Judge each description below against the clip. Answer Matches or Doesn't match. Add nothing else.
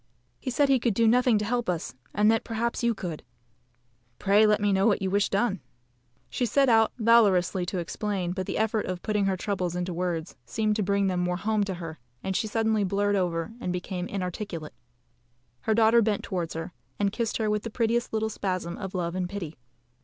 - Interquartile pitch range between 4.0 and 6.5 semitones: Doesn't match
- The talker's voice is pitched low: Doesn't match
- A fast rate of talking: Matches